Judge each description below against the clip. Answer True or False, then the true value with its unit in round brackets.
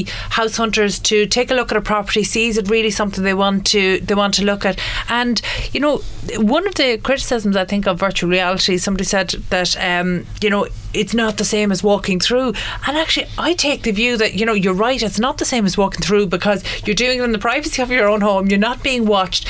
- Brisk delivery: True (245 wpm)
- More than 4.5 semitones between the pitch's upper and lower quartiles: False (3.3 semitones)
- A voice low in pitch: False (210 Hz)